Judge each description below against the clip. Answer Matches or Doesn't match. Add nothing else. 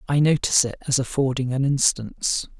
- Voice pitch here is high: Doesn't match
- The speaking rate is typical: Matches